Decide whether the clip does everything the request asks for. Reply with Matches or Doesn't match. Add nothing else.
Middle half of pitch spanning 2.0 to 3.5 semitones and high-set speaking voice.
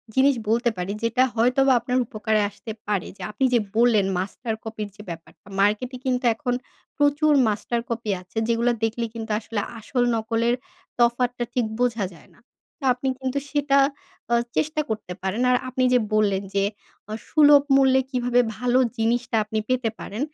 Matches